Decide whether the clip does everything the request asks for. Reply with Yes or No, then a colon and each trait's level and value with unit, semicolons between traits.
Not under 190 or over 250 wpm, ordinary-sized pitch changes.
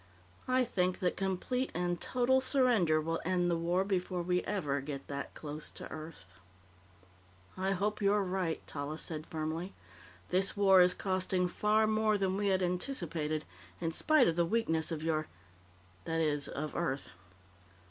No: average, 155 wpm; average, 3.8 semitones